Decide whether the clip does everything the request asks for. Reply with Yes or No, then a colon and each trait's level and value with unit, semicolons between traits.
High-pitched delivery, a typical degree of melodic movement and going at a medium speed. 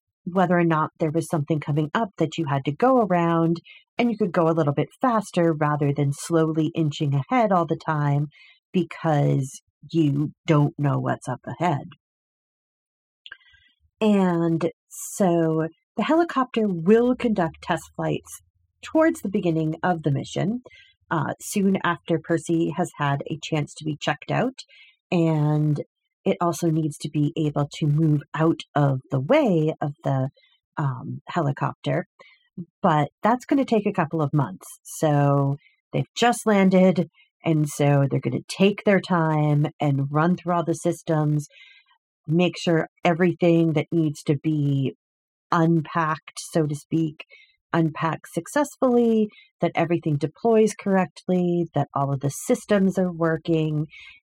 No: medium, 165 Hz; average, 4.2 semitones; average, 145 wpm